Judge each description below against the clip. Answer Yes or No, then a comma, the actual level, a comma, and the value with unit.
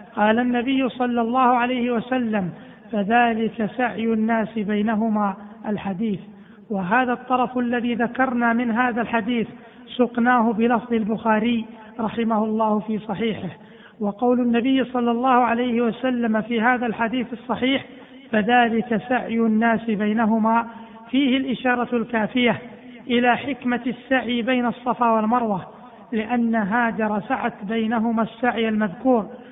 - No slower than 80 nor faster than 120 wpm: Yes, average, 110 wpm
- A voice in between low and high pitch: No, high, 235 Hz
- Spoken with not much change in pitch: Yes, narrow, 1.8 semitones